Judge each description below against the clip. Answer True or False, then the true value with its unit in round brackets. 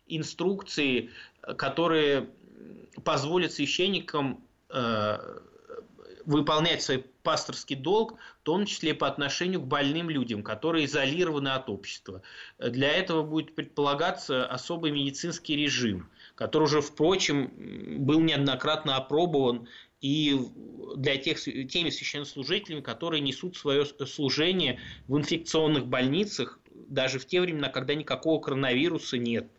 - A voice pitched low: False (150 Hz)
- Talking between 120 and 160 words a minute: False (110 wpm)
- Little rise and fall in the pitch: False (3.5 semitones)